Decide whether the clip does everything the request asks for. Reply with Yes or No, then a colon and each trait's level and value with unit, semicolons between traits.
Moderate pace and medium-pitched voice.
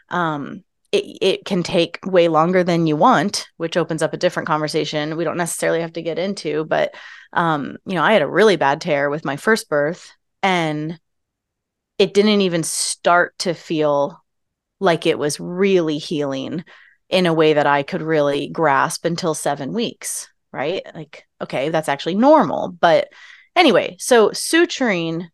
Yes: average, 165 wpm; medium, 165 Hz